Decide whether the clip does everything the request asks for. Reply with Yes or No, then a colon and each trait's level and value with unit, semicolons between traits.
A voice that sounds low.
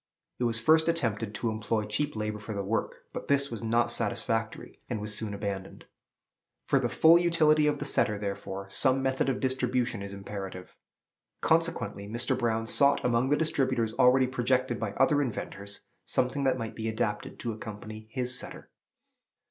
Yes: low, 115 Hz